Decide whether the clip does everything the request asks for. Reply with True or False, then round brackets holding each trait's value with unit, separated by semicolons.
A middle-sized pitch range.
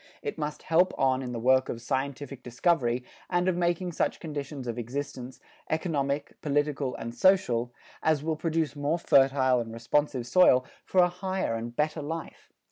True (4.4 semitones)